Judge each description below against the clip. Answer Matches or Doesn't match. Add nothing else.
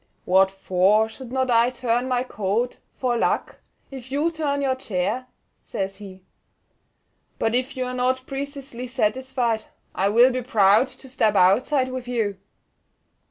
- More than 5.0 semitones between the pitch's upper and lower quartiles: Doesn't match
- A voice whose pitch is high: Matches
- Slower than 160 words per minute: Matches